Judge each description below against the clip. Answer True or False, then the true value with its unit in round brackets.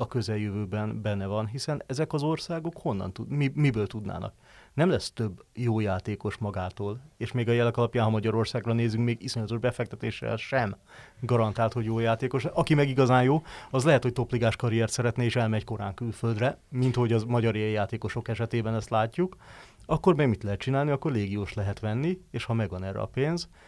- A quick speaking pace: True (180 wpm)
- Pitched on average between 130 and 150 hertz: False (115 Hz)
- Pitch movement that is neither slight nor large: True (3.4 semitones)